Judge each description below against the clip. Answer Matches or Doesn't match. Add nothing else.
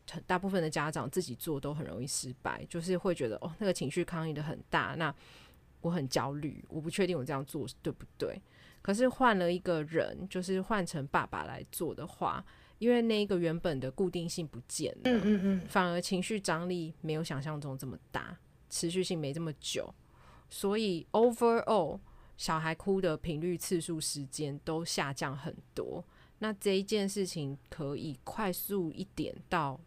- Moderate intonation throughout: Matches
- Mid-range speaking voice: Matches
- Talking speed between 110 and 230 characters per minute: Doesn't match